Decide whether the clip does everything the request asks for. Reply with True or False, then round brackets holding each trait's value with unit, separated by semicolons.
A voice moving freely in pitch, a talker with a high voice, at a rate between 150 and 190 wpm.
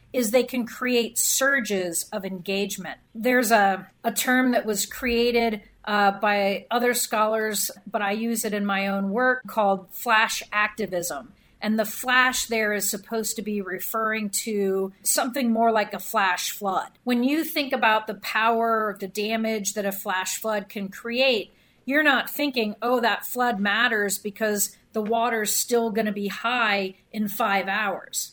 False (2.8 semitones; 220 Hz; 165 wpm)